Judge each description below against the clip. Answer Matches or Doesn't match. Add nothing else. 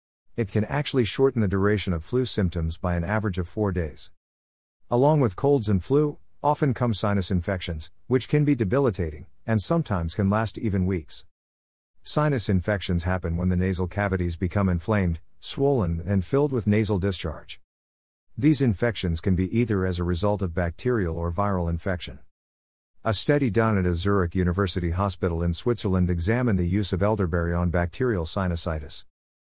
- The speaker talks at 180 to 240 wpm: Doesn't match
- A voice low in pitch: Matches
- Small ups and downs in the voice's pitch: Doesn't match